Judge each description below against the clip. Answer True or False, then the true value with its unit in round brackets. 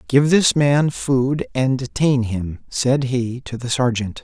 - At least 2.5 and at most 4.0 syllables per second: True (3.6 syllables/s)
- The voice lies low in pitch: True (130 Hz)